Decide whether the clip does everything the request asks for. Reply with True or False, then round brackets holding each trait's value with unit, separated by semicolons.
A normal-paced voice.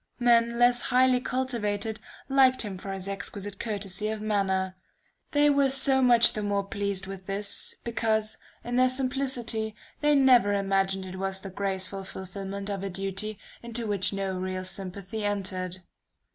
True (155 wpm)